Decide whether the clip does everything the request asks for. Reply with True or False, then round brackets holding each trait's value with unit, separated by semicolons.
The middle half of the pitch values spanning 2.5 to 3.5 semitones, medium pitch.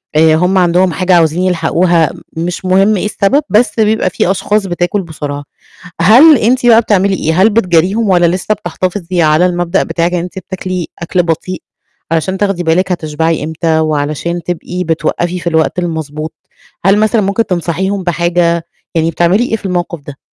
True (2.8 semitones; 175 Hz)